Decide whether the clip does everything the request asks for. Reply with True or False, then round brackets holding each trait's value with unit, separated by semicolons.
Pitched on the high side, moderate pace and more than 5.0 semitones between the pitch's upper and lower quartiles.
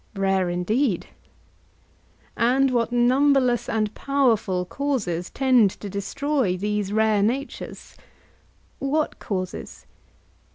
False (225 Hz; 90 wpm; 5.4 semitones)